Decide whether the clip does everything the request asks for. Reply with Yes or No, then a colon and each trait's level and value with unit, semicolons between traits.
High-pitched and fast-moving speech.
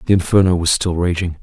No: very low, 90 Hz; fast, 210 wpm